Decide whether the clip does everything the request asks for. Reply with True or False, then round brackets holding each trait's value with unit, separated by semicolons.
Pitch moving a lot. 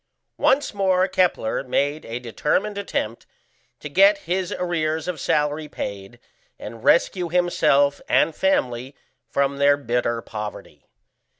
True (6.5 semitones)